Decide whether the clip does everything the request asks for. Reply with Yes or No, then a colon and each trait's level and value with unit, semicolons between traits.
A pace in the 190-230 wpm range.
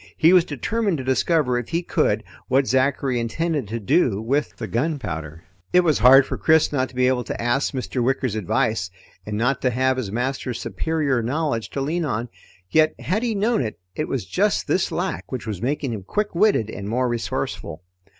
Yes: average, 200 wpm